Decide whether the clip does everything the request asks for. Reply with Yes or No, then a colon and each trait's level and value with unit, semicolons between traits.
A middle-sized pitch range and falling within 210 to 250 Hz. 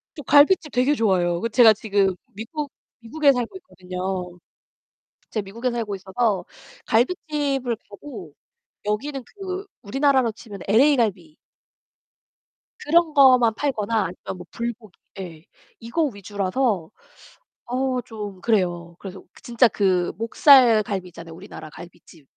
No: wide, 5.8 semitones; high, 225 Hz